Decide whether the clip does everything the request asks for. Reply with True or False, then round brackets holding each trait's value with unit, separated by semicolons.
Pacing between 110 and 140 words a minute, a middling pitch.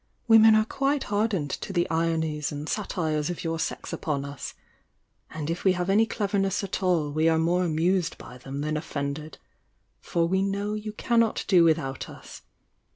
False (175 wpm; 170 Hz)